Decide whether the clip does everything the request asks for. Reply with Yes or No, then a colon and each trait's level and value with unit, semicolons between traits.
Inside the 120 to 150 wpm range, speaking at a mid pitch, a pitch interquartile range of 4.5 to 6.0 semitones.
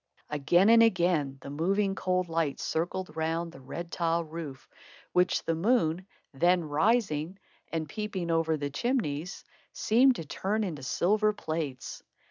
No: average, 140 wpm; medium, 170 Hz; average, 3.7 semitones